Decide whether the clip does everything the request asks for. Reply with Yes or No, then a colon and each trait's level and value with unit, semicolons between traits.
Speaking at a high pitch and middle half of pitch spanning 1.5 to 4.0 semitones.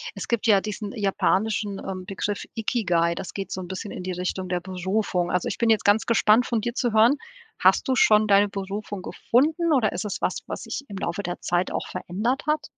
Yes: high, 205 Hz; average, 3.3 semitones